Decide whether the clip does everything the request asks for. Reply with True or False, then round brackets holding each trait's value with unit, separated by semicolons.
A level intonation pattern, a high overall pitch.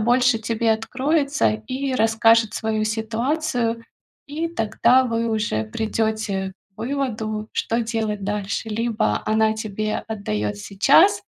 True (2.3 semitones; 225 Hz)